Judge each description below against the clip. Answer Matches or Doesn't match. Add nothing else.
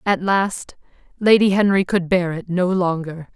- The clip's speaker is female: Matches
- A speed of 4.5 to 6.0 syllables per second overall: Doesn't match